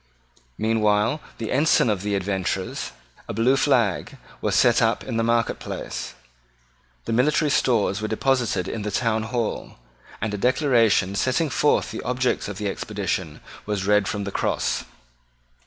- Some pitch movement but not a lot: Yes, average, 3.6 semitones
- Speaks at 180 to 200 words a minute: No, average, 150 wpm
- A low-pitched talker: Yes, low, 110 Hz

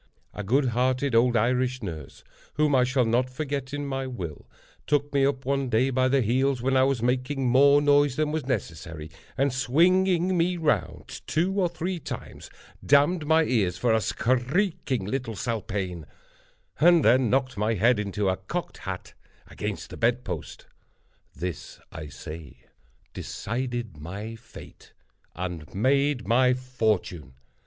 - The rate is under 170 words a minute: Yes, average, 150 wpm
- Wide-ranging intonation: No, average, 4.6 semitones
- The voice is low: Yes, low, 130 Hz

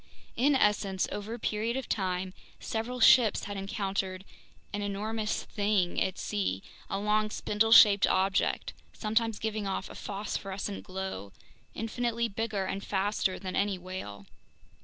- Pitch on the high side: Yes, high, 205 Hz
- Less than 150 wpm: Yes, average, 140 wpm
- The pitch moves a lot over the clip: No, narrow, 2.4 semitones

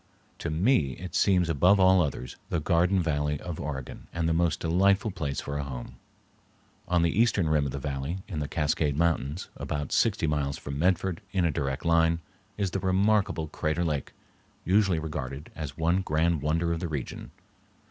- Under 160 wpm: No, average, 185 wpm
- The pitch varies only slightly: No, average, 3.6 semitones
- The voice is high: No, very low, 80 Hz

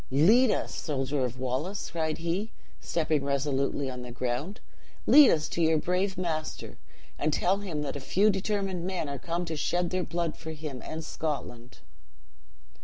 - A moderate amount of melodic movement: Yes, average, 4.6 semitones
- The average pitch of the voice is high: No, medium, 160 Hz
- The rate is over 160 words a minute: Yes, average, 170 wpm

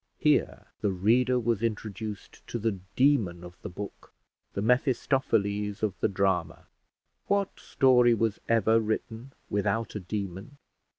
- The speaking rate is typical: No, slow, 130 wpm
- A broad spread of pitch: No, average, 3.1 semitones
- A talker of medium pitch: No, low, 110 Hz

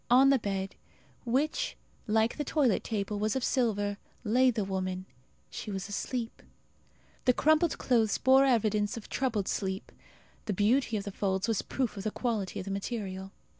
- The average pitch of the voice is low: No, high, 215 Hz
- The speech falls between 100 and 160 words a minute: No, average, 170 wpm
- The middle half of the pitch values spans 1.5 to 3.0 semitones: No, average, 4.1 semitones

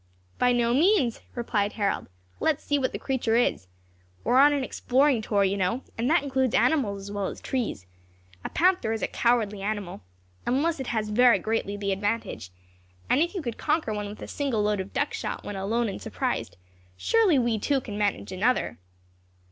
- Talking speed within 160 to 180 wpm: No, average, 195 wpm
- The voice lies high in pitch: Yes, high, 230 Hz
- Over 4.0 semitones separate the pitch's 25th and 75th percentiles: Yes, average, 4.7 semitones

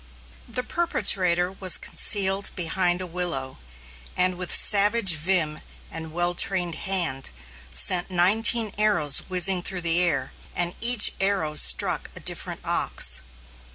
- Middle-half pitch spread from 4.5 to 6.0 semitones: No, narrow, 2.5 semitones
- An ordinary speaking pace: No, slow, 125 wpm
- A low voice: No, medium, 180 Hz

